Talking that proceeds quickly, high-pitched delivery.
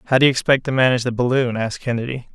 No: fast, 255 wpm; low, 125 Hz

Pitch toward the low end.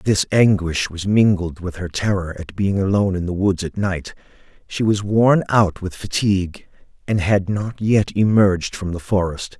Yes: very low, 95 Hz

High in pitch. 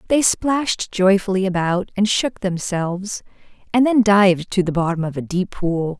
Yes: high, 195 Hz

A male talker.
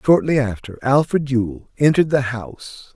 Yes: male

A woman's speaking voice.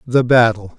No: male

